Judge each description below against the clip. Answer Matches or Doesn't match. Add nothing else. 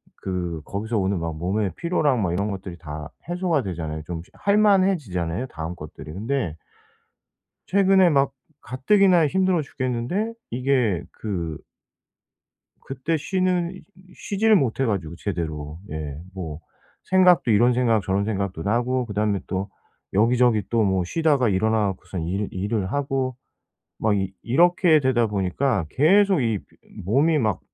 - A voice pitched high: Doesn't match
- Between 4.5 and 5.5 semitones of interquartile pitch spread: Doesn't match